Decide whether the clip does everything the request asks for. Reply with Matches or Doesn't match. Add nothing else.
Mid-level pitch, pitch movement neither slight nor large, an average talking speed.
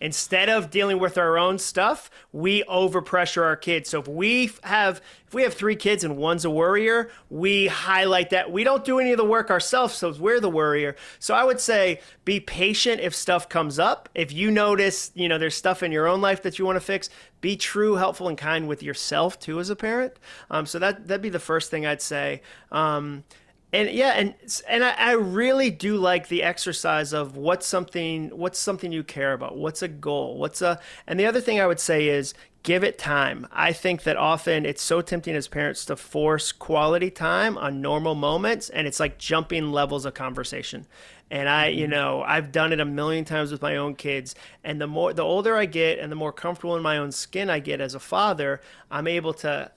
Doesn't match